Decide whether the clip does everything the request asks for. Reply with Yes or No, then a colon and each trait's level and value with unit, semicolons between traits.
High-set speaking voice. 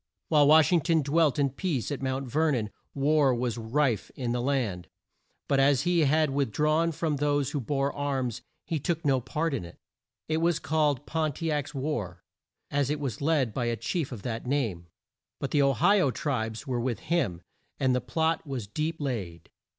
No: medium, 140 Hz